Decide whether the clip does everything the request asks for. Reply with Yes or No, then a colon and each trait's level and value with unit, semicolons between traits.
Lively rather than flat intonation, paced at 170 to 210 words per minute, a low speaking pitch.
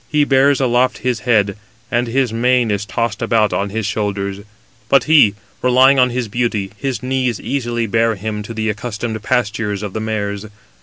No: average, 3.3 semitones; average, 190 wpm; low, 115 Hz